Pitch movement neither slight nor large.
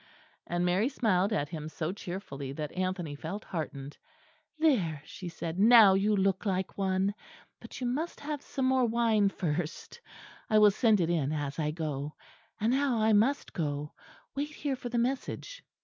No: wide, 6.5 semitones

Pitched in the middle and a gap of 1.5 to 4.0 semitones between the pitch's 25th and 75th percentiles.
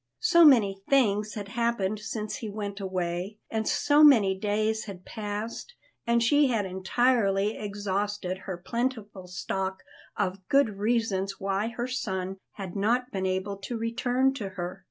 No: high, 205 Hz; average, 3.4 semitones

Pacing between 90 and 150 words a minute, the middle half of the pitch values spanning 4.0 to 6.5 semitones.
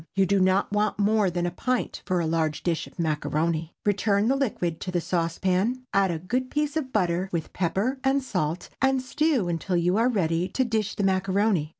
No: fast, 205 wpm; average, 4.7 semitones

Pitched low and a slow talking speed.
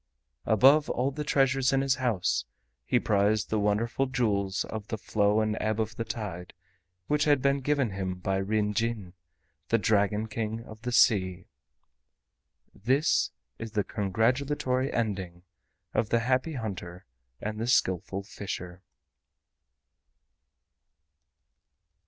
Yes: low, 110 Hz; slow, 130 wpm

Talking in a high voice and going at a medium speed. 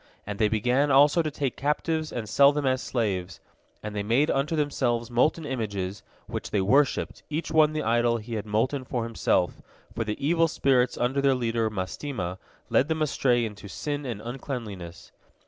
No: low, 125 Hz; average, 180 wpm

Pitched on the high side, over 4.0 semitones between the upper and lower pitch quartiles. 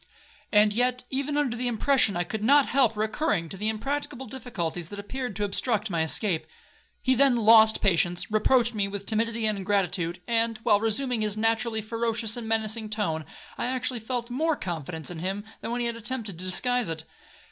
No: high, 220 Hz; average, 3.5 semitones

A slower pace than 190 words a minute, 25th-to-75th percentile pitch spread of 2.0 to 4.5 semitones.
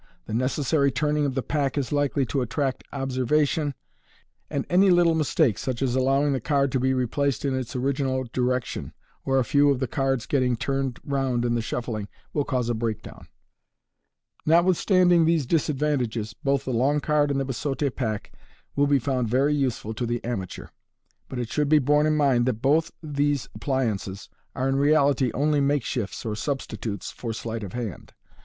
Yes: average, 180 wpm; average, 3.0 semitones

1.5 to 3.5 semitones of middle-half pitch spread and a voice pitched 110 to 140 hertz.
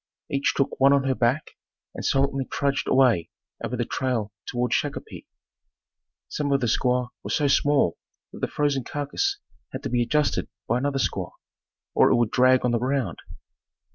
Yes: narrow, 2.4 semitones; low, 135 Hz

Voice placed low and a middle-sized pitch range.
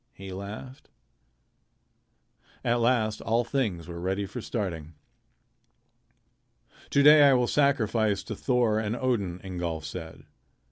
Yes: low, 110 Hz; average, 5.0 semitones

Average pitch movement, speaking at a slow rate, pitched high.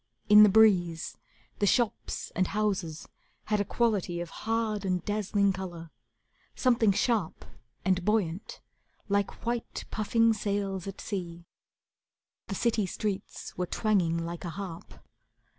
Yes: average, 3.3 semitones; slow, 125 wpm; high, 200 Hz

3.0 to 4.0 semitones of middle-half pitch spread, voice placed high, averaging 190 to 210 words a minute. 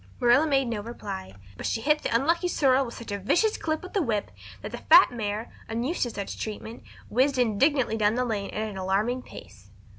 No: average, 4.4 semitones; high, 235 Hz; fast, 205 wpm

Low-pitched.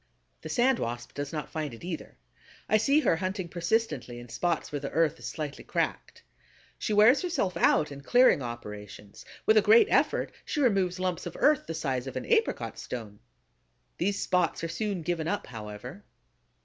No: medium, 170 Hz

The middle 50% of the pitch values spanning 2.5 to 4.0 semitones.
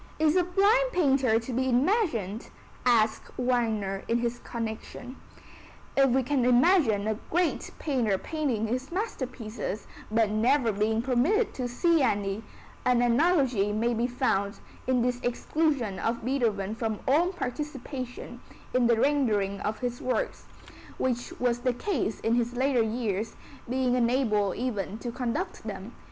Yes: average, 3.5 semitones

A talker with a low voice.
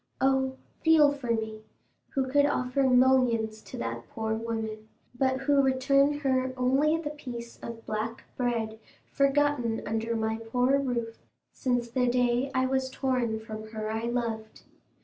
No: high, 245 Hz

